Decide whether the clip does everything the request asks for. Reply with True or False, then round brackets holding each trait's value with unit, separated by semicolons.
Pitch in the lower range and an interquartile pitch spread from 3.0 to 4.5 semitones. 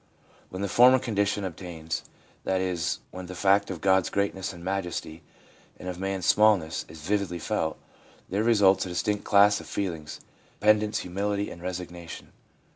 False (95 Hz; 2.5 semitones)